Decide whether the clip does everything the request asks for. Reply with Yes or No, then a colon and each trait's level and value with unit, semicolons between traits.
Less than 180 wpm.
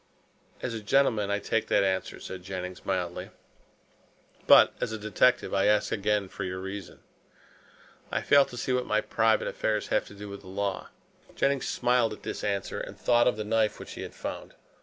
No: average, 195 wpm